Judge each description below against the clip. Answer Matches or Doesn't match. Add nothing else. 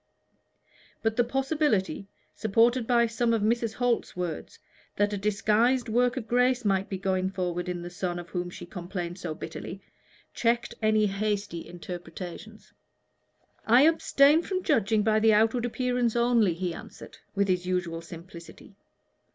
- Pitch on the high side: Matches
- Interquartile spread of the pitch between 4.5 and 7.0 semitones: Matches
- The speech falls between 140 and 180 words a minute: Matches